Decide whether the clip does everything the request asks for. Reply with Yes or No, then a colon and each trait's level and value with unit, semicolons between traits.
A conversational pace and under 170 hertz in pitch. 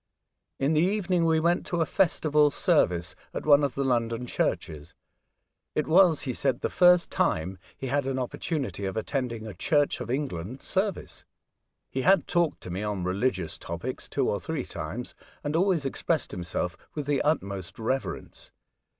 Yes: average, 165 wpm; low, 135 Hz